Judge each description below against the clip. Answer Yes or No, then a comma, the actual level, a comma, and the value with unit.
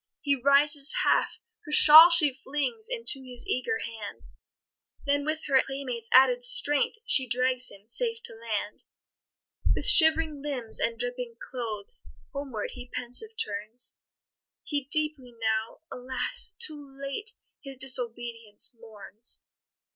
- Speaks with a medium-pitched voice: No, very high, 265 Hz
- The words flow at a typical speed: No, slow, 125 wpm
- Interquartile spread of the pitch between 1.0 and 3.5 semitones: No, average, 4.0 semitones